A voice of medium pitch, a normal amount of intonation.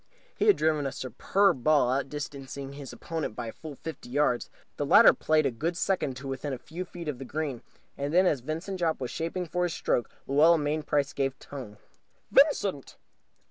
Yes: medium, 145 Hz; average, 3.5 semitones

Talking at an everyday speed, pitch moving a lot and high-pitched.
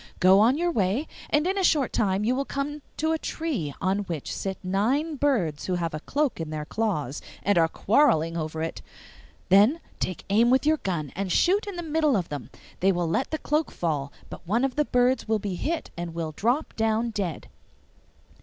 No: fast, 210 wpm; wide, 9.0 semitones; high, 215 Hz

